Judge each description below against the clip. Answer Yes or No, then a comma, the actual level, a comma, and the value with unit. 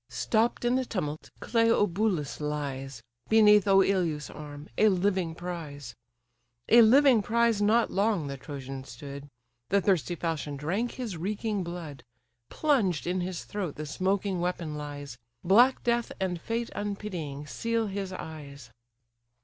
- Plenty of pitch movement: Yes, wide, 6.1 semitones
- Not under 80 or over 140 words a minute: Yes, slow, 135 wpm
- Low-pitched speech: No, medium, 180 Hz